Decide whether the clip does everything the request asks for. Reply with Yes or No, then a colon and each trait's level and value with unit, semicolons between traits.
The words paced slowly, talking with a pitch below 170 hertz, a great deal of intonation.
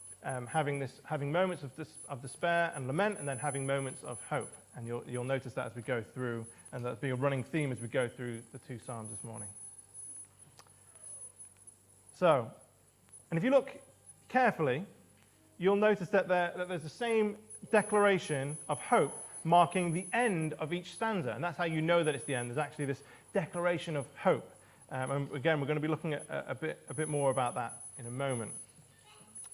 No: average, 200 wpm; medium, 140 Hz; wide, 6.2 semitones